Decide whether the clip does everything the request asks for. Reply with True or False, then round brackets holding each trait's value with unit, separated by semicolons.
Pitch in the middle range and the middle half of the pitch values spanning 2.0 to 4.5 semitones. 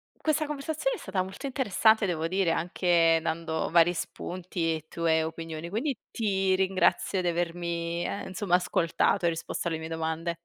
True (175 Hz; 2.7 semitones)